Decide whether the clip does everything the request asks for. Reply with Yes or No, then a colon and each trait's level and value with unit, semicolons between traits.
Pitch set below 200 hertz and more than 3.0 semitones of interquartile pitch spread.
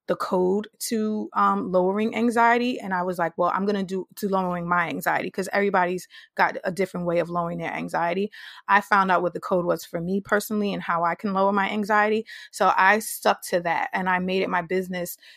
No: high, 190 Hz; average, 2.7 semitones